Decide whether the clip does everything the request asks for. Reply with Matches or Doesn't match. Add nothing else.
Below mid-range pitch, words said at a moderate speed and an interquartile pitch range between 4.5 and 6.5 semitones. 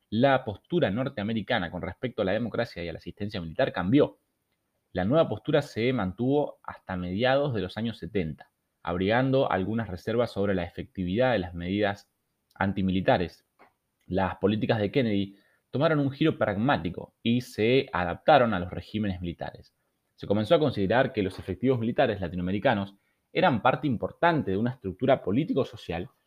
Matches